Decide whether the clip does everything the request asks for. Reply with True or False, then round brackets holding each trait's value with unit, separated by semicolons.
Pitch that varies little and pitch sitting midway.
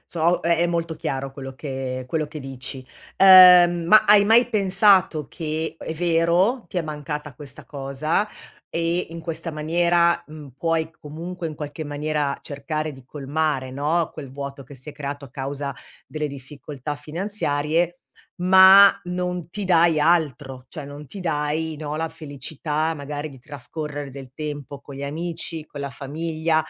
False (3.1 semitones; 155 Hz)